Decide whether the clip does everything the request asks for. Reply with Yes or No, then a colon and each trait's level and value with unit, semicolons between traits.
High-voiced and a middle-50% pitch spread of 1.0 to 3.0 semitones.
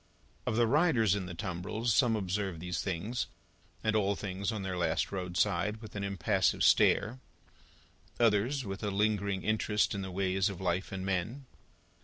No: low, 100 Hz; average, 2.7 semitones